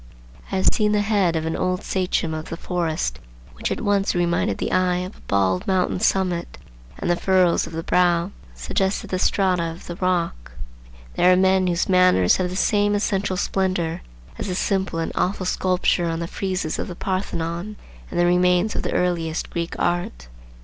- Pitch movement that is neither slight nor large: No, narrow, 2.0 semitones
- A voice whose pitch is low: No, medium, 180 Hz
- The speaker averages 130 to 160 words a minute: No, average, 190 wpm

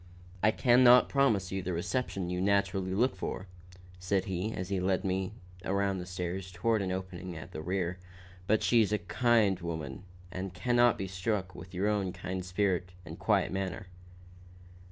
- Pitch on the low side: Yes, very low, 95 Hz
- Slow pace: No, average, 185 wpm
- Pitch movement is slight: Yes, narrow, 2.2 semitones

